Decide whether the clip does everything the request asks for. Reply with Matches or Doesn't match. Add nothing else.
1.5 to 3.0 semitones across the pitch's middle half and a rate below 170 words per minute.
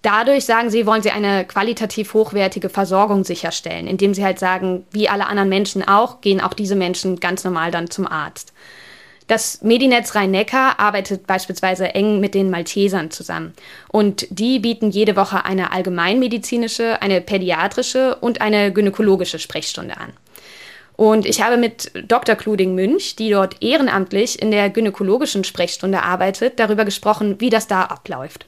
Matches